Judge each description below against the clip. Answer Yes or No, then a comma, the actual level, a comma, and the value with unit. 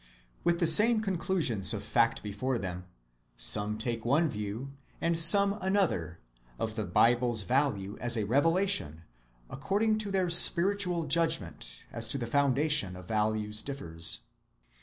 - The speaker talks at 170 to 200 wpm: No, average, 140 wpm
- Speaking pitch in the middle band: No, low, 130 Hz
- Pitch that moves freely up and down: Yes, wide, 8.2 semitones